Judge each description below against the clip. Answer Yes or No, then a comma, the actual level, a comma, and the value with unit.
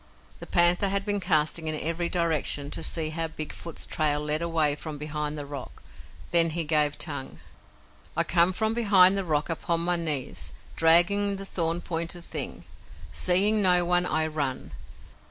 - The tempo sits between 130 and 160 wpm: No, average, 170 wpm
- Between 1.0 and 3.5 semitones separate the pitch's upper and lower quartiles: Yes, narrow, 2.6 semitones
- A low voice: No, medium, 165 Hz